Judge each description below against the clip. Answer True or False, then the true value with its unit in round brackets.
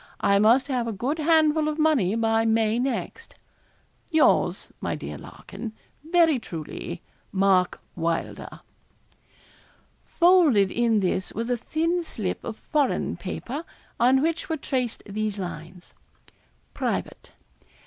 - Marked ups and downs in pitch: True (7.4 semitones)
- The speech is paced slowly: True (120 wpm)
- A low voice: False (235 Hz)